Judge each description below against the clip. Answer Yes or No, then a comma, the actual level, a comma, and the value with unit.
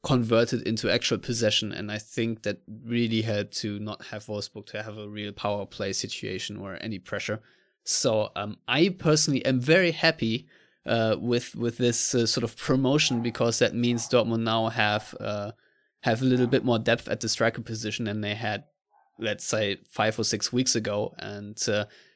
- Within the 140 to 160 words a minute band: No, average, 185 wpm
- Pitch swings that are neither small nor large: No, narrow, 2.3 semitones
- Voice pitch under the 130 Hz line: Yes, low, 115 Hz